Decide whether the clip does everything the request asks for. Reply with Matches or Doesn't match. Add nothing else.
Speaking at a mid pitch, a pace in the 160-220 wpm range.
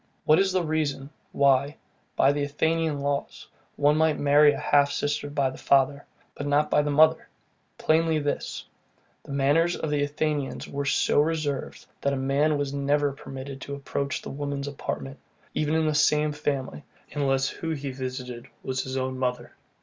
Matches